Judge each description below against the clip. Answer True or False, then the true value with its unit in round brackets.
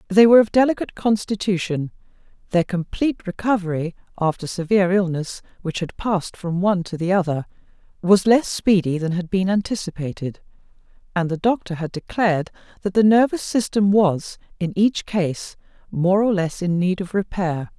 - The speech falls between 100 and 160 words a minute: True (155 wpm)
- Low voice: False (185 Hz)